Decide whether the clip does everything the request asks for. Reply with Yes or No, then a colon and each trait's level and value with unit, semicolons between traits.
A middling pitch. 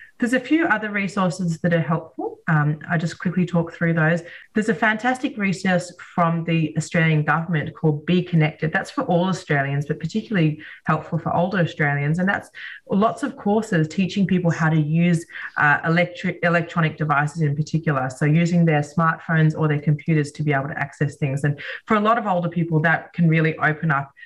Yes: medium, 165 Hz